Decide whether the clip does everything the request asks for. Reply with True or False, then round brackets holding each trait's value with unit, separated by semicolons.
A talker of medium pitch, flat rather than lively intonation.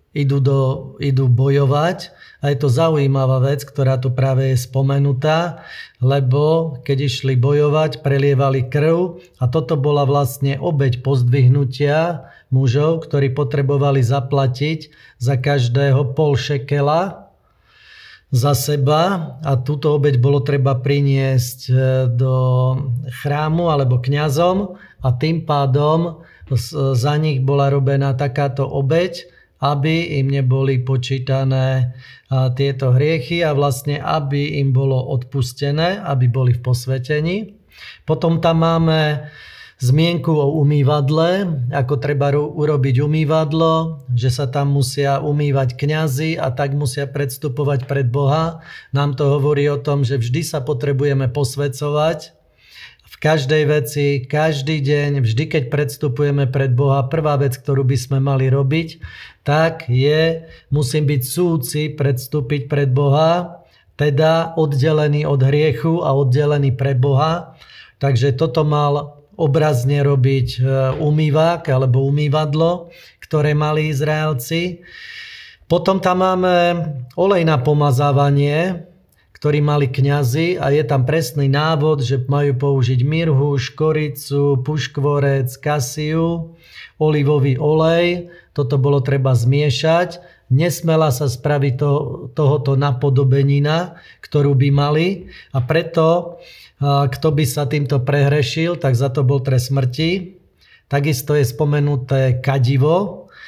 True (145 Hz; 2.3 semitones)